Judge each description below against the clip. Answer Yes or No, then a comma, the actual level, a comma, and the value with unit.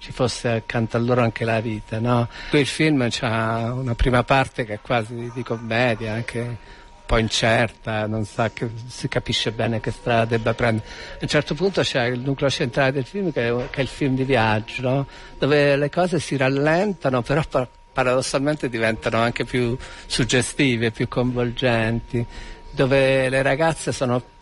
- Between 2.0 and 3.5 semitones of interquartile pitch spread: Yes, average, 3.0 semitones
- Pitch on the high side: No, low, 125 Hz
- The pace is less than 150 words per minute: No, average, 165 wpm